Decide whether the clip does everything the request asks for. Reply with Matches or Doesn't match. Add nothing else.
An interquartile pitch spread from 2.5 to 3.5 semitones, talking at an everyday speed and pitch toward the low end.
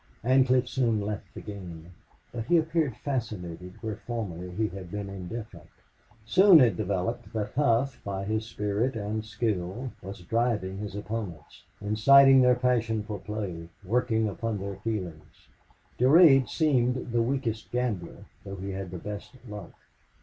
Doesn't match